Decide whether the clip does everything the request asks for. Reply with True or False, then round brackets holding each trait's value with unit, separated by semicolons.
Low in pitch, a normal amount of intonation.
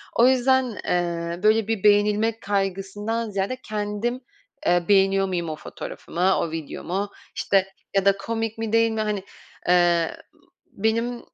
False (205 Hz; 3.1 semitones)